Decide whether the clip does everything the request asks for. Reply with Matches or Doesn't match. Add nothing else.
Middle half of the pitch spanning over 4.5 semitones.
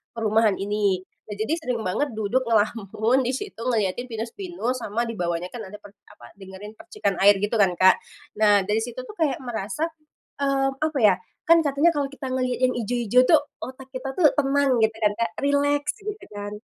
Matches